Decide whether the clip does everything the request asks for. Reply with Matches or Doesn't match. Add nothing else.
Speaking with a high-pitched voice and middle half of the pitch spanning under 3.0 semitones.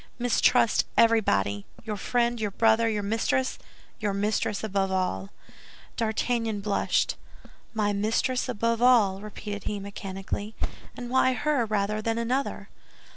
Matches